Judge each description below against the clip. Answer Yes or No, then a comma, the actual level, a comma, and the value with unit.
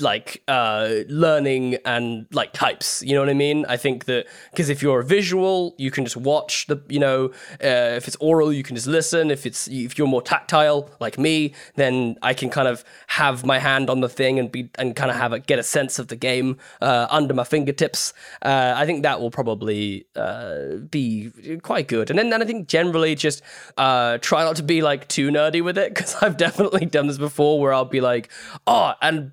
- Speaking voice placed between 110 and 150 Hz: Yes, medium, 140 Hz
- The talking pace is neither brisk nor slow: No, fast, 225 wpm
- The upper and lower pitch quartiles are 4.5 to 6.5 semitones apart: No, average, 3.4 semitones